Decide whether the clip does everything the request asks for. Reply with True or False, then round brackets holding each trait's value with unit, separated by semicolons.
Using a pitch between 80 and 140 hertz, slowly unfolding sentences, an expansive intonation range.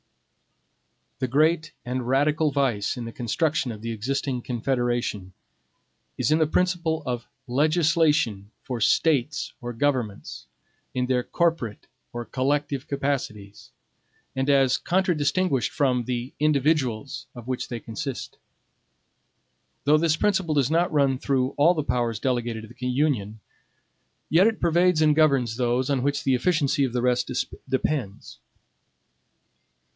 False (135 Hz; 130 wpm; 4.1 semitones)